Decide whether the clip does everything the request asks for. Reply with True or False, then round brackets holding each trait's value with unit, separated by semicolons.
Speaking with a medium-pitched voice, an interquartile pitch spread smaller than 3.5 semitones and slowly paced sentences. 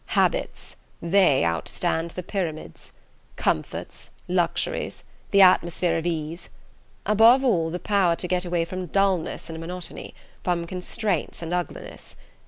True (175 Hz; 2.4 semitones; 125 wpm)